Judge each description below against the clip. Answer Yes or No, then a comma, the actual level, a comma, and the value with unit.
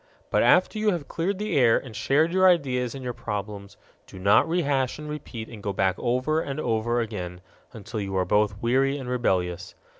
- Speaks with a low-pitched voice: Yes, low, 125 Hz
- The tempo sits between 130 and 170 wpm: No, average, 200 wpm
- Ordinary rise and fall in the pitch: No, wide, 5.9 semitones